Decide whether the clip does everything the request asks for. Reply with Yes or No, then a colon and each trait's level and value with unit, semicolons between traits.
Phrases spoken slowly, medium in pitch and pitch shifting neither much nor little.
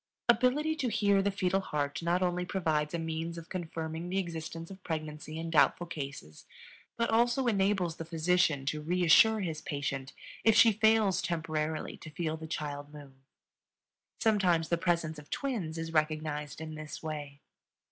No: average, 160 wpm; medium, 165 Hz; average, 3.8 semitones